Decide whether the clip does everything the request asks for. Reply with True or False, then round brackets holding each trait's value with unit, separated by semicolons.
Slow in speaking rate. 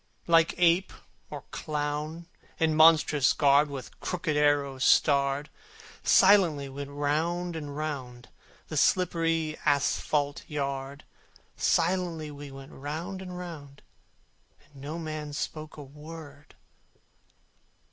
True (110 wpm)